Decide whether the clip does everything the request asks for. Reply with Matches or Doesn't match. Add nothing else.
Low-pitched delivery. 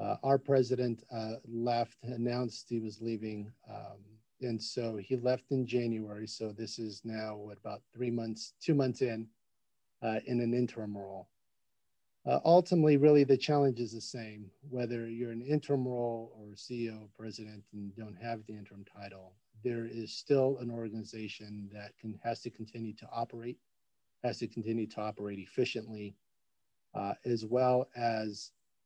Matches